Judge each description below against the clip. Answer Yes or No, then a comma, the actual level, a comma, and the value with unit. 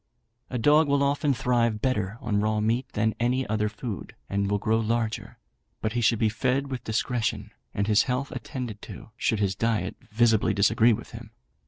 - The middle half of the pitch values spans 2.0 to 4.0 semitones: Yes, average, 2.9 semitones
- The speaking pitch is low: Yes, low, 115 Hz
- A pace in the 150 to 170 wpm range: No, average, 190 wpm